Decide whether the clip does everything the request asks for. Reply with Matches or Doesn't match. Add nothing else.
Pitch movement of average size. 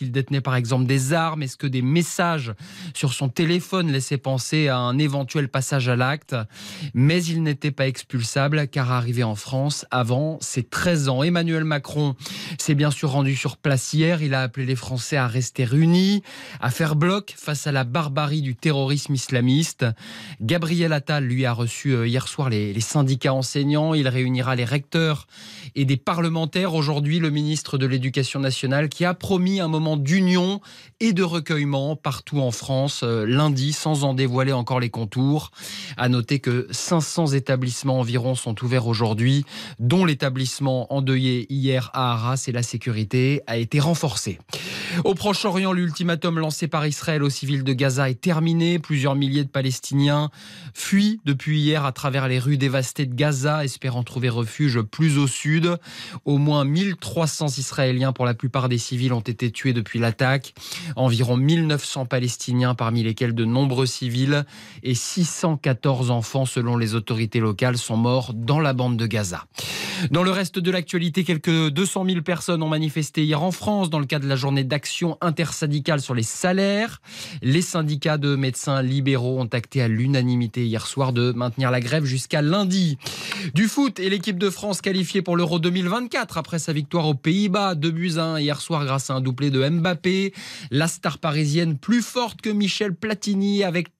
Matches